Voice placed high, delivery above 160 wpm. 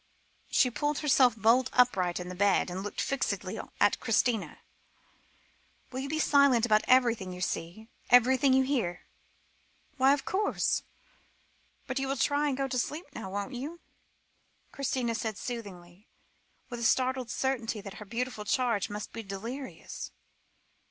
No: high, 245 Hz; average, 150 wpm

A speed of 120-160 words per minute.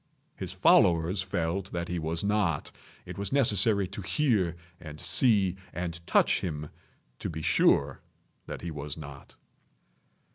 Yes: average, 140 wpm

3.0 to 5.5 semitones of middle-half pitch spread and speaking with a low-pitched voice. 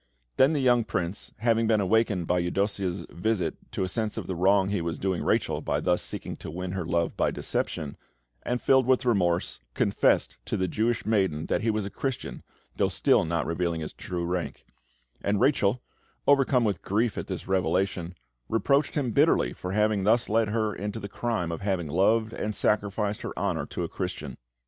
Yes: average, 4.2 semitones; low, 100 Hz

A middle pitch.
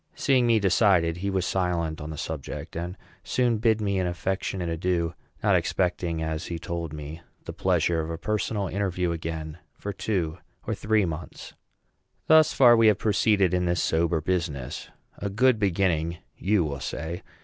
No: very low, 90 Hz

